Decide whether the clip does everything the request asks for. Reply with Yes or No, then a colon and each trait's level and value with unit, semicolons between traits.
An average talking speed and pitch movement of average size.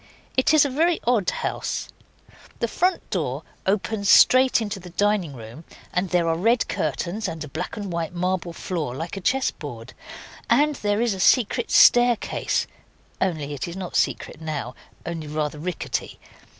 No: average, 165 wpm; wide, 5.8 semitones